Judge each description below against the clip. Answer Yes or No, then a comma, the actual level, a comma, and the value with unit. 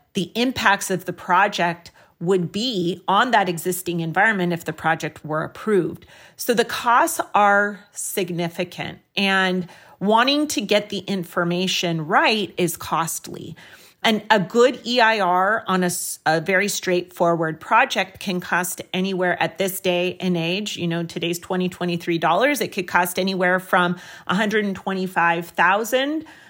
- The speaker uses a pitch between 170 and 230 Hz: Yes, medium, 185 Hz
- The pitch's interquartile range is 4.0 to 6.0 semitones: No, average, 2.8 semitones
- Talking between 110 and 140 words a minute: Yes, slow, 135 wpm